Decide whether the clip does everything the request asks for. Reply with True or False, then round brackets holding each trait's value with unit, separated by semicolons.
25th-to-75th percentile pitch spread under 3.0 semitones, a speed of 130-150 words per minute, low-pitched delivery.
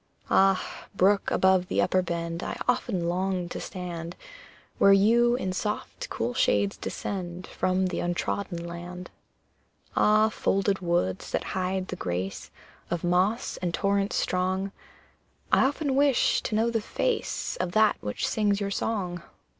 False (2.6 semitones; 145 wpm; 185 Hz)